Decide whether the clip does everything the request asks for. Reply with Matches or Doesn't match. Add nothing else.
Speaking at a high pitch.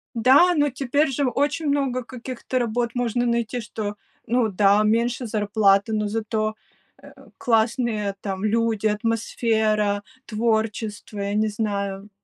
Matches